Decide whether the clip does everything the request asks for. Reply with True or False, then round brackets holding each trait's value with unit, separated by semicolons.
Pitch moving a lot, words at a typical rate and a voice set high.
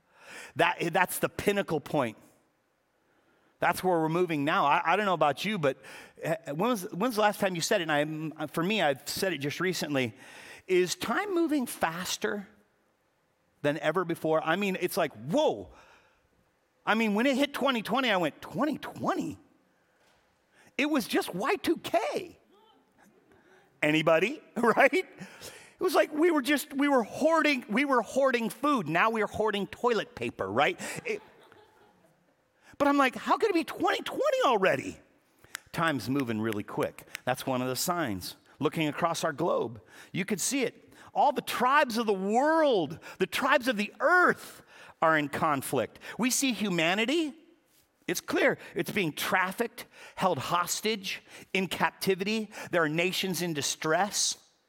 True (8.9 semitones; 150 wpm; 200 Hz)